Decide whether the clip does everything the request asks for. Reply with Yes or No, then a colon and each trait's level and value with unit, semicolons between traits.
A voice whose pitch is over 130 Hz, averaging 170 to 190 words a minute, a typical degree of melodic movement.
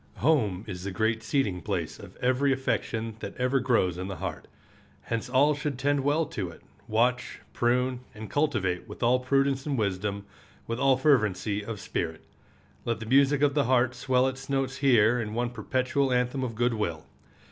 No: low, 125 Hz; average, 180 wpm; average, 4.0 semitones